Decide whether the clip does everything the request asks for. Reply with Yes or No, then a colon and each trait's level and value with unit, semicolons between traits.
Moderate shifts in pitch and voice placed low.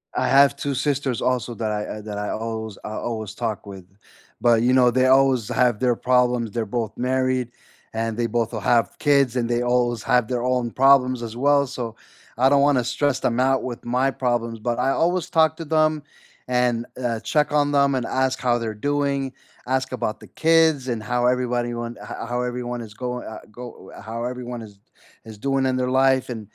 No: narrow, 2.3 semitones; low, 125 Hz